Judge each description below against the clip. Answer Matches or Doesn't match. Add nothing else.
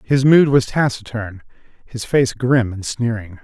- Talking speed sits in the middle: Matches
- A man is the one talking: Matches